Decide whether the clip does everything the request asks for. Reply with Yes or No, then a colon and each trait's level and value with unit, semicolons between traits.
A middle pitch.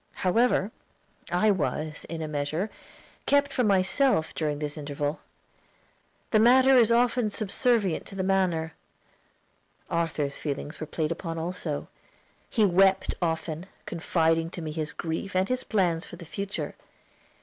Yes: medium, 175 Hz